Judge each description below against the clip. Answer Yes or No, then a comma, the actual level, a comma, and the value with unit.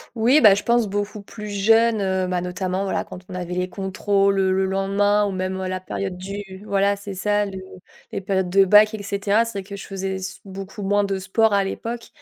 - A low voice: No, high, 195 Hz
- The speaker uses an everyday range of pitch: No, narrow, 1.4 semitones